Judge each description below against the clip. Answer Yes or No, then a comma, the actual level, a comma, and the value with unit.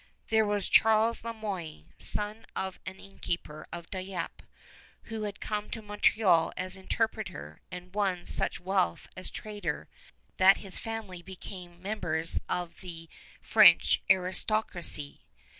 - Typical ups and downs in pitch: Yes, average, 3.3 semitones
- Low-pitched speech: No, high, 190 Hz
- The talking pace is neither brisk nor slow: No, slow, 125 wpm